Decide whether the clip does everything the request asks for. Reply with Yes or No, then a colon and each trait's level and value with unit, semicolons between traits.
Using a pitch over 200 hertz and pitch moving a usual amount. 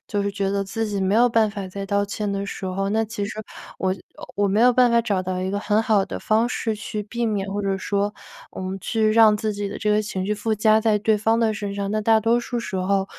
No: high, 210 Hz; narrow, 1.8 semitones